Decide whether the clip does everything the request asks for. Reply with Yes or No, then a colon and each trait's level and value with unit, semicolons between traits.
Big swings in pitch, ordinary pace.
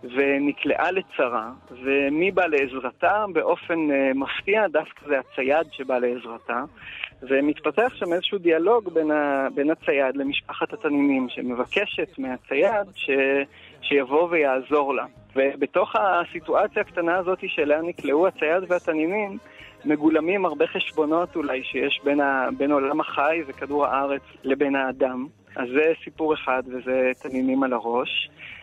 No: average, 4.0 semitones; average, 120 wpm